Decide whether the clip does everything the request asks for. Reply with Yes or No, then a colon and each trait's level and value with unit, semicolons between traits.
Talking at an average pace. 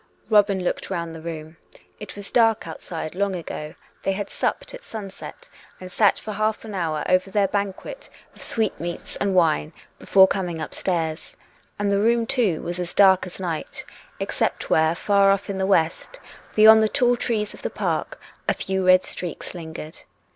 Yes: average, 175 wpm